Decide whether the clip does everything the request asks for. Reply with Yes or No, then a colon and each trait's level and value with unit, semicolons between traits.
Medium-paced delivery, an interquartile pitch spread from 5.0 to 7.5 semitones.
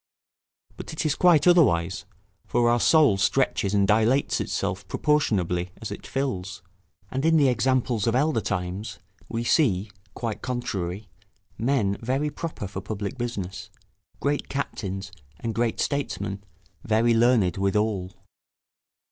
No: slow, 130 wpm; average, 5.3 semitones